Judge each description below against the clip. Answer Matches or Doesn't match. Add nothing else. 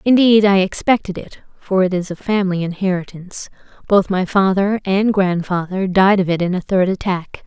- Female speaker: Matches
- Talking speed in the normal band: Matches